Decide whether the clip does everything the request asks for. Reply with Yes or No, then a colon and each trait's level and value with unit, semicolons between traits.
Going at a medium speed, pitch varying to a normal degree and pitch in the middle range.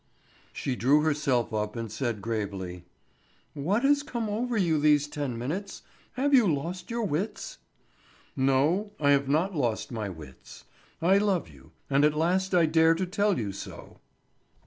No: average, 160 wpm; wide, 8.0 semitones; medium, 150 Hz